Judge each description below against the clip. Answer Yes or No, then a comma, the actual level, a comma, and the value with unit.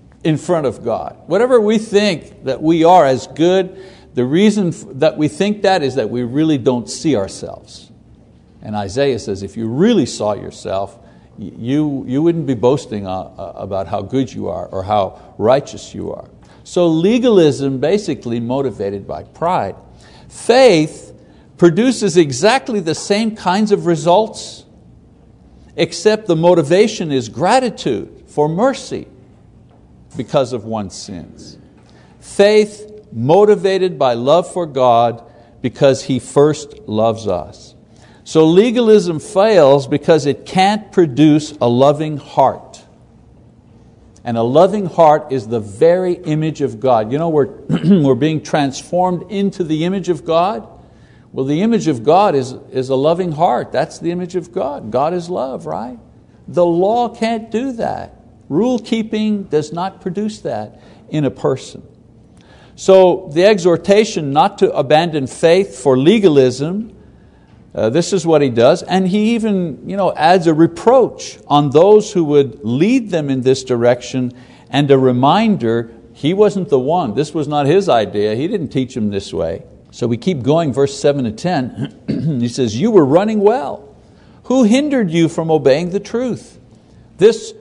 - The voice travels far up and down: Yes, wide, 6.7 semitones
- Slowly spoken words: No, average, 150 wpm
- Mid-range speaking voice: Yes, medium, 155 Hz